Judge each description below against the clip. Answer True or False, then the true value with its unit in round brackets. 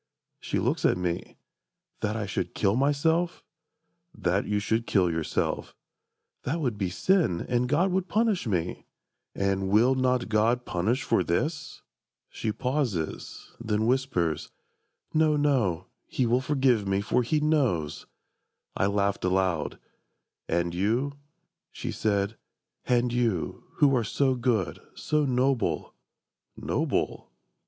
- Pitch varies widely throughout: True (5.7 semitones)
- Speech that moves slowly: True (125 wpm)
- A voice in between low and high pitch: False (115 Hz)